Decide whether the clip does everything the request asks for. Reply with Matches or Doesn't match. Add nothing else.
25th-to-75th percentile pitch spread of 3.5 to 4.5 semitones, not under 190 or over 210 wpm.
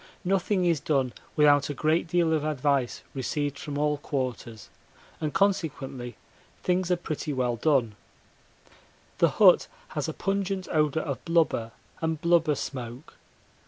Doesn't match